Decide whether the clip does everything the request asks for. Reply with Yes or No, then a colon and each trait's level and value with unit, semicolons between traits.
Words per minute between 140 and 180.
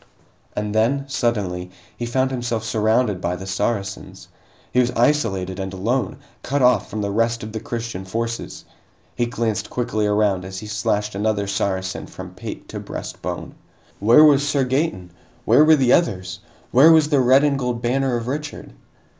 Yes: average, 170 wpm